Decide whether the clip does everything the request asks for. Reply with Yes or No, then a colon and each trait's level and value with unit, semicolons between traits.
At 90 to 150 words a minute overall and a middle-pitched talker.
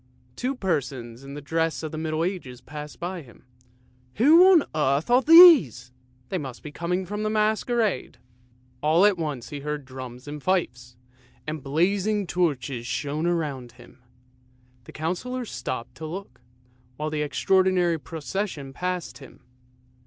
Yes: average, 145 wpm; medium, 155 Hz